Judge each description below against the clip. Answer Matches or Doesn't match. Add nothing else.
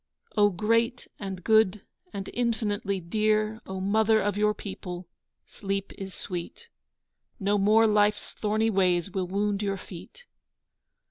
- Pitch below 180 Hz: Doesn't match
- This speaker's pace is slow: Matches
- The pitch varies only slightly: Matches